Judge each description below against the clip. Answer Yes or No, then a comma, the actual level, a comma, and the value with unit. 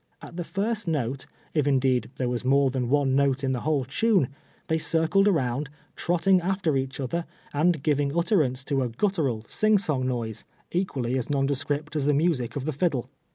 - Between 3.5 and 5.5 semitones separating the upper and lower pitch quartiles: Yes, average, 4.4 semitones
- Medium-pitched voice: Yes, medium, 145 Hz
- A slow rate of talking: No, average, 185 wpm